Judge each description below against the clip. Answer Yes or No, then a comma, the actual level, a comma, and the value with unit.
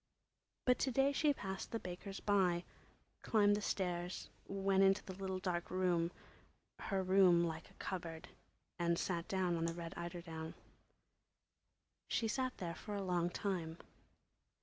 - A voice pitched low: No, medium, 185 Hz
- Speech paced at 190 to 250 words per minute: No, average, 140 wpm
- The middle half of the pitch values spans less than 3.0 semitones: Yes, narrow, 2.4 semitones